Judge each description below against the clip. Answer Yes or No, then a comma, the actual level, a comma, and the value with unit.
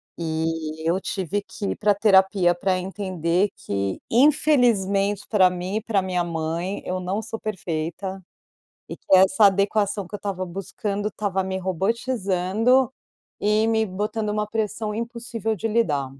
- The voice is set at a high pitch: Yes, high, 195 Hz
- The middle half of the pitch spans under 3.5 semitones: Yes, average, 2.8 semitones